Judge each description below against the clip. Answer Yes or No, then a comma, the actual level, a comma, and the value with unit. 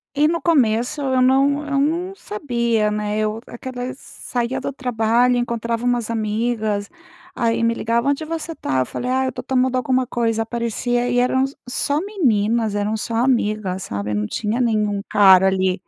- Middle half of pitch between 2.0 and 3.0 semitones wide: No, average, 3.4 semitones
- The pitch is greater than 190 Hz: Yes, high, 235 Hz